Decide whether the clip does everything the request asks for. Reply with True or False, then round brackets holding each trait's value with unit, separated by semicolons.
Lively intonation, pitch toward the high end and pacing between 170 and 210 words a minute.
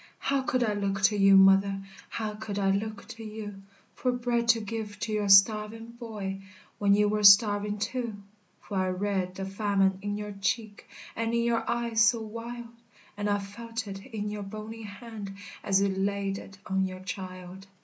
False (2.4 semitones; 205 Hz; 185 wpm)